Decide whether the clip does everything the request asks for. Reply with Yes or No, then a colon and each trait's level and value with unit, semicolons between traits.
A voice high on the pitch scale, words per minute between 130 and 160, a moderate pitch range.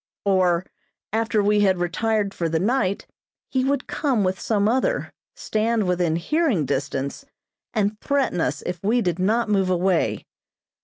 Yes: high, 200 Hz; average, 150 wpm; average, 4.2 semitones